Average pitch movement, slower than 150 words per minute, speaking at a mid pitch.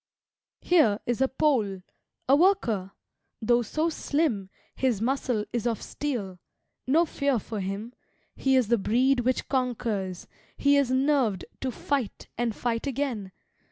No: average, 4.5 semitones; average, 140 wpm; high, 245 Hz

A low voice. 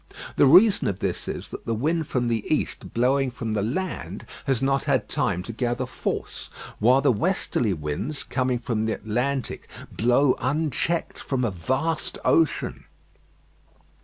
Yes: low, 125 Hz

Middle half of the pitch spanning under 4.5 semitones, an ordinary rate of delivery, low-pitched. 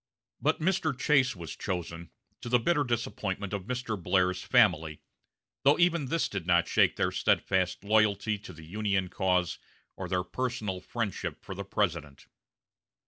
No: average, 5.3 semitones; average, 150 wpm; low, 100 Hz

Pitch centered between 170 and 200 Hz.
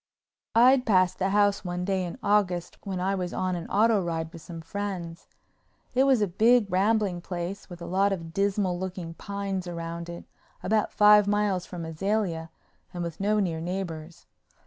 Yes: medium, 185 Hz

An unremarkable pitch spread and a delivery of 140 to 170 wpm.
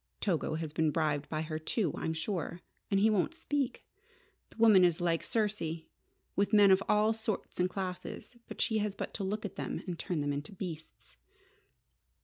No: average, 4.7 semitones; average, 180 wpm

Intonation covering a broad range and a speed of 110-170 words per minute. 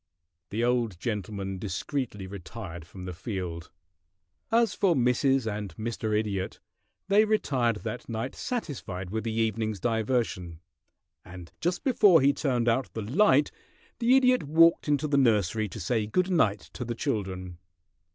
Yes: wide, 6.0 semitones; average, 145 wpm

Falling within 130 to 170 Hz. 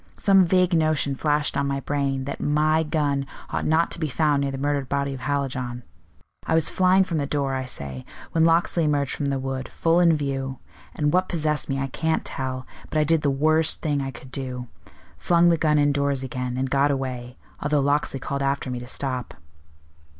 Yes: medium, 140 Hz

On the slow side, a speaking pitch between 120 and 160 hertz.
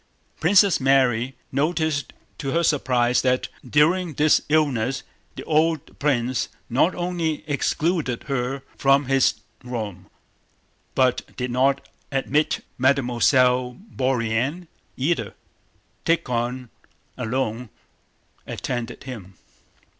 Yes: slow, 95 wpm; low, 135 Hz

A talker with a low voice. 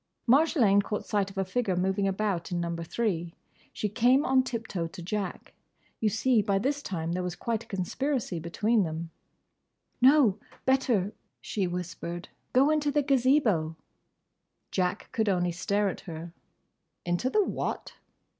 No: high, 200 Hz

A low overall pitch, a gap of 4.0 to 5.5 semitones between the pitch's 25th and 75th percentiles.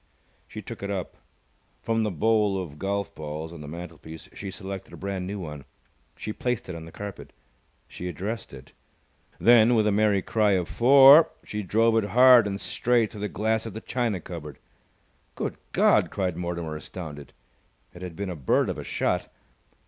Yes: low, 100 Hz; average, 4.3 semitones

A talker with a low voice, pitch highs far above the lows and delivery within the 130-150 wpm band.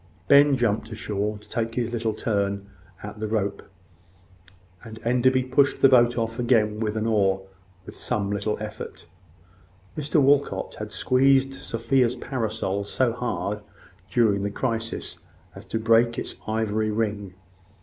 No: low, 115 Hz; average, 2.8 semitones; average, 140 wpm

